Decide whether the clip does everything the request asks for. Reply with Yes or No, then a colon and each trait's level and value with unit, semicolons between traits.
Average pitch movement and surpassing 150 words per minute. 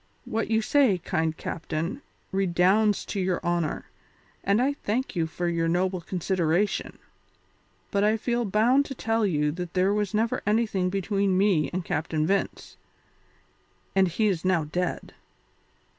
No: average, 3.6 semitones; average, 145 wpm